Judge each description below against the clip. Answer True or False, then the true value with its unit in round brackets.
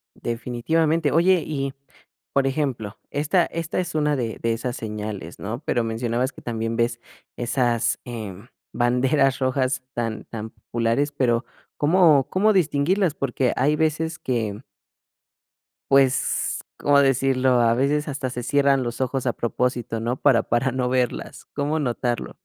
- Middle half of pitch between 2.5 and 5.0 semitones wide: True (3.5 semitones)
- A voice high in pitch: False (130 Hz)